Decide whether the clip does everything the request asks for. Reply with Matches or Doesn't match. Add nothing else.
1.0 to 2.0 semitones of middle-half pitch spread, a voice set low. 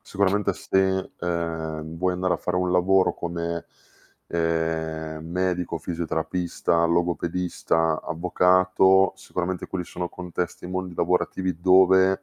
Matches